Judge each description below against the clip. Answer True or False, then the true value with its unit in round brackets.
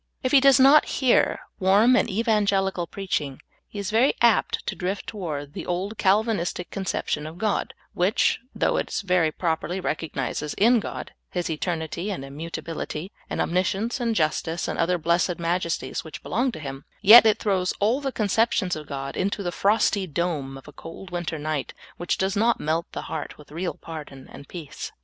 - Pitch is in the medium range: True (180 Hz)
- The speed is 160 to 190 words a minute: True (180 wpm)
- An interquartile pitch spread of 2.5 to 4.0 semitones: False (4.7 semitones)